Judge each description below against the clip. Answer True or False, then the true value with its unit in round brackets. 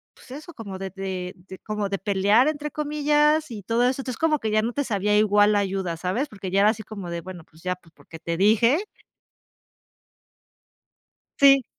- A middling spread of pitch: False (5.9 semitones)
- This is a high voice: True (210 Hz)